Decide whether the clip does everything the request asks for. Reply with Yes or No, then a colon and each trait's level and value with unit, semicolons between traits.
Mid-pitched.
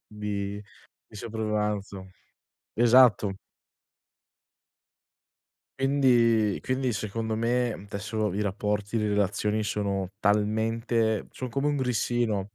No: low, 110 Hz